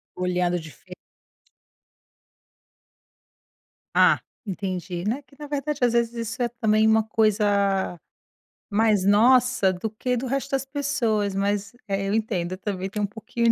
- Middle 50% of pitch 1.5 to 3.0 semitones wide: No, average, 3.5 semitones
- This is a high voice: Yes, high, 215 Hz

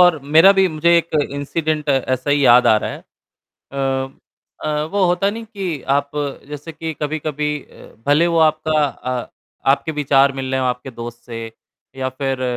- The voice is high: No, medium, 145 Hz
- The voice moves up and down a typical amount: Yes, average, 3.1 semitones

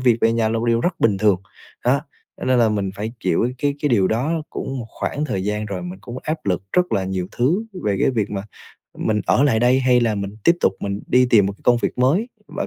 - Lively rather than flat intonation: No, average, 4.2 semitones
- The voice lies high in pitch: No, low, 115 Hz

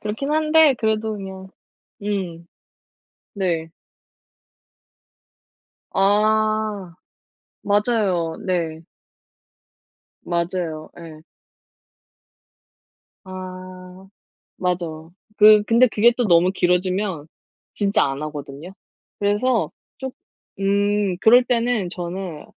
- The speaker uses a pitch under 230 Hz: Yes, high, 190 Hz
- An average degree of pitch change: Yes, average, 3.7 semitones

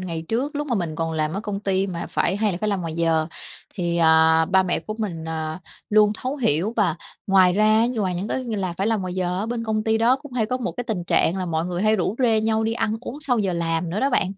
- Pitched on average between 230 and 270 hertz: No, high, 195 Hz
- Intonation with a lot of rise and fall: No, average, 4.5 semitones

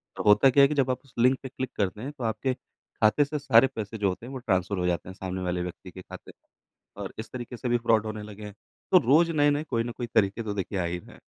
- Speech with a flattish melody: No, average, 4.9 semitones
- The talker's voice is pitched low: Yes, low, 115 Hz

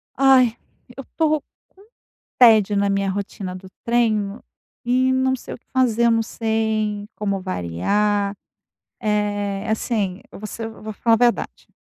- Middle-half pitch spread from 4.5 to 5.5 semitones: No, average, 2.9 semitones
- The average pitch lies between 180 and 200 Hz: No, high, 215 Hz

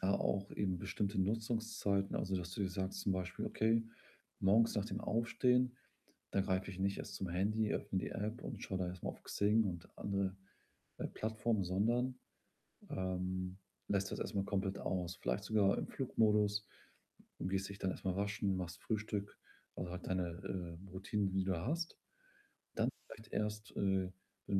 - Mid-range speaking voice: No, low, 100 Hz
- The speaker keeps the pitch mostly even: Yes, narrow, 2.3 semitones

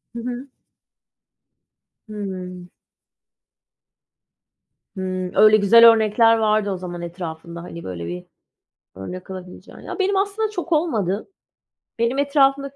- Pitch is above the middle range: Yes, high, 210 Hz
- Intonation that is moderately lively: No, wide, 6.8 semitones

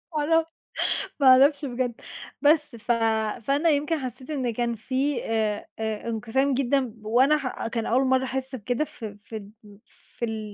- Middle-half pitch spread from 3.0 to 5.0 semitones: Yes, average, 3.6 semitones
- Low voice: No, very high, 255 Hz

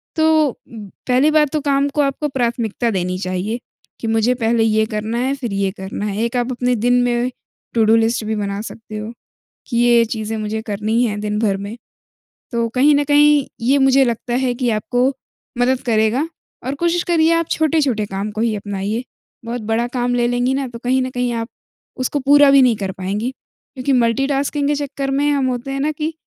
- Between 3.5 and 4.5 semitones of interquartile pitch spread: Yes, average, 3.8 semitones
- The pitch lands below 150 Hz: No, high, 245 Hz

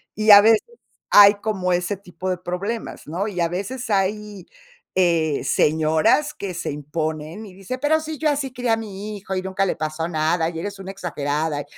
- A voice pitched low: No, high, 190 Hz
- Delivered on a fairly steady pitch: No, average, 4.4 semitones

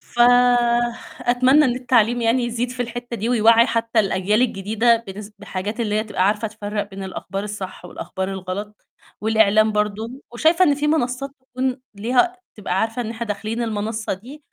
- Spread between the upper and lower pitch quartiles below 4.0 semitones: Yes, average, 2.9 semitones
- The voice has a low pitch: No, high, 225 Hz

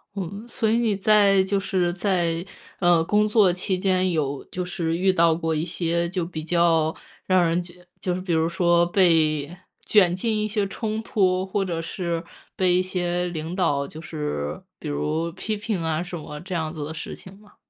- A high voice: No, medium, 175 Hz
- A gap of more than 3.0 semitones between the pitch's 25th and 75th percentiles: No, narrow, 2.6 semitones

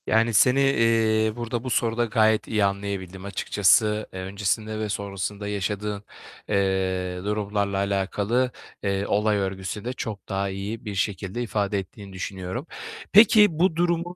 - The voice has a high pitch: No, low, 105 Hz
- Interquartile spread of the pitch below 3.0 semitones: Yes, narrow, 2.6 semitones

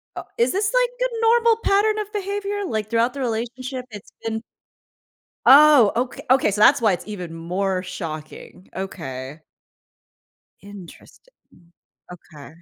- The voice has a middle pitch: No, high, 230 Hz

